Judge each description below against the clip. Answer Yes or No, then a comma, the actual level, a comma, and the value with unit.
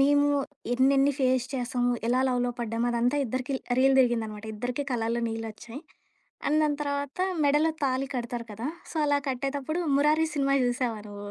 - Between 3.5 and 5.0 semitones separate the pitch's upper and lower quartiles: No, average, 3.1 semitones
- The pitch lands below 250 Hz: No, very high, 255 Hz